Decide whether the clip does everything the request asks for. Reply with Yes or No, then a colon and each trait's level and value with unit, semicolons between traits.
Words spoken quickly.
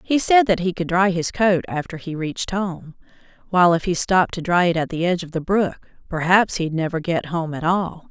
Yes: fast, 235 wpm